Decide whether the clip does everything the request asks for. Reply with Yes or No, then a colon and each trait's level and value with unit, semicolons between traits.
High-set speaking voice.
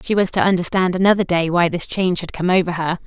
No: medium, 180 Hz